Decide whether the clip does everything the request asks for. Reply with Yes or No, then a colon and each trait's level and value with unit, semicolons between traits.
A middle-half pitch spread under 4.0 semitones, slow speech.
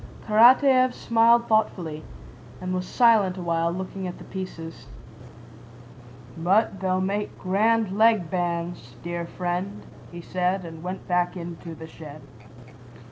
Yes: average, 3.5 semitones; slow, 125 wpm